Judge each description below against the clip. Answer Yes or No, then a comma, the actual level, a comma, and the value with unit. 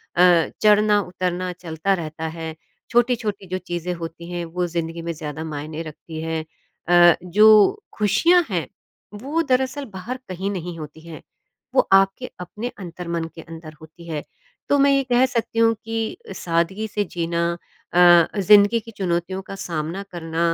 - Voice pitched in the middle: Yes, medium, 180 Hz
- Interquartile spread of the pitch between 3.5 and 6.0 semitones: Yes, average, 4.2 semitones